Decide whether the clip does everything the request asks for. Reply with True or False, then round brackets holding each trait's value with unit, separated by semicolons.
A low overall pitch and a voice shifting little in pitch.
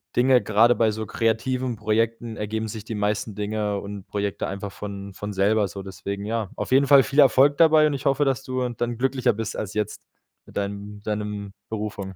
False (110 Hz; 3.3 semitones)